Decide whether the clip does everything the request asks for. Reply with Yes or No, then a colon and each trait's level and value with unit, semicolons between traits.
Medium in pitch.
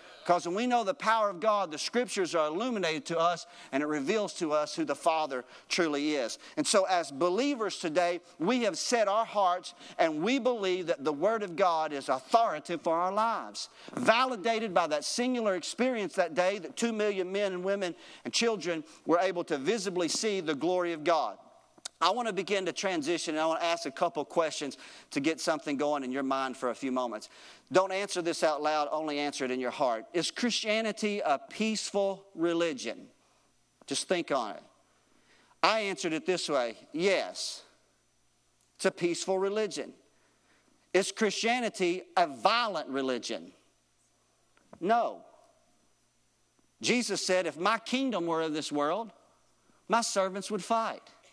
Yes: medium, 180 Hz